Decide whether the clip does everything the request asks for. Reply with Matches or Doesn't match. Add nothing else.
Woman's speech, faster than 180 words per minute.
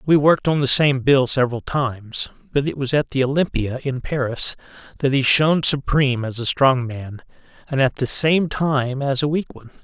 Doesn't match